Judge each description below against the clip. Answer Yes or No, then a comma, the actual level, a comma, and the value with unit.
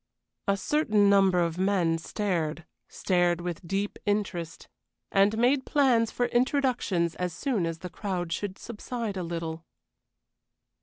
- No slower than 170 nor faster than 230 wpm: No, slow, 135 wpm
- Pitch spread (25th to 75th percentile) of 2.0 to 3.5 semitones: No, average, 4.4 semitones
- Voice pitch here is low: No, high, 195 Hz